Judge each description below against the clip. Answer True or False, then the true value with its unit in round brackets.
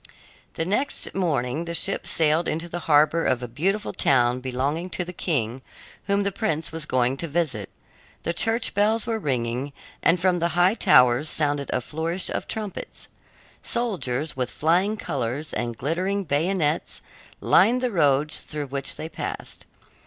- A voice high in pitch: False (160 Hz)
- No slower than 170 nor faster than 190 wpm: False (160 wpm)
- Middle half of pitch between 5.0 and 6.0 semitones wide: True (5.4 semitones)